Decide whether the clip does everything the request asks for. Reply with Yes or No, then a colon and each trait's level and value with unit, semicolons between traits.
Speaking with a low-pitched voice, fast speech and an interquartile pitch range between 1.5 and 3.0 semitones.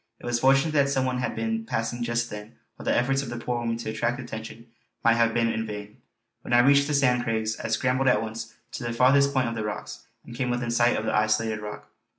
Yes: low, 120 Hz; fast, 255 wpm; narrow, 2.4 semitones